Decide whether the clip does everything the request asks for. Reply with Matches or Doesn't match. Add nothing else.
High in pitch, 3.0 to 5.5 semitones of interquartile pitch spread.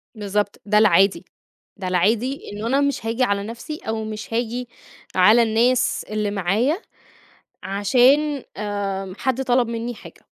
Matches